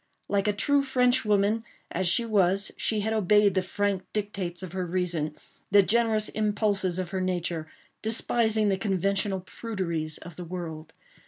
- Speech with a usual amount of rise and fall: Yes, average, 3.1 semitones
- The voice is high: Yes, high, 195 Hz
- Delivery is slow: No, average, 145 wpm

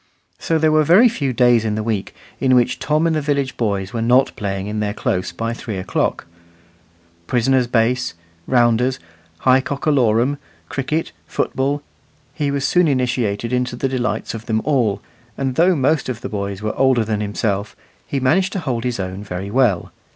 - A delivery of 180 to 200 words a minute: Yes, average, 185 wpm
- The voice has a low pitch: Yes, low, 125 Hz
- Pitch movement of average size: Yes, average, 4.3 semitones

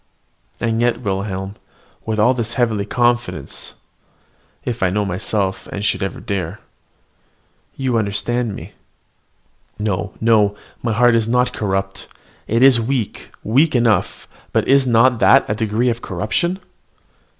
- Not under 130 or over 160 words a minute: Yes, average, 140 wpm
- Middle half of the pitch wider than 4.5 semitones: No, average, 3.1 semitones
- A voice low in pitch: Yes, low, 115 Hz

